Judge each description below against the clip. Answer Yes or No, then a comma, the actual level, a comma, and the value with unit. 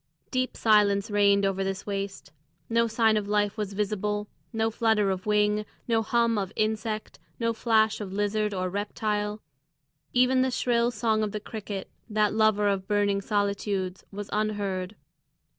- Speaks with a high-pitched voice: Yes, high, 210 Hz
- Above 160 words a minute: No, average, 155 wpm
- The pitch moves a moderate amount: No, narrow, 1.6 semitones